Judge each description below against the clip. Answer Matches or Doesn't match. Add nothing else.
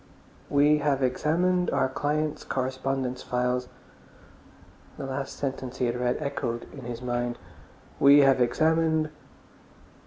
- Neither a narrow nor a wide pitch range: Matches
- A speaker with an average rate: Doesn't match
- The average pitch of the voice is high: Doesn't match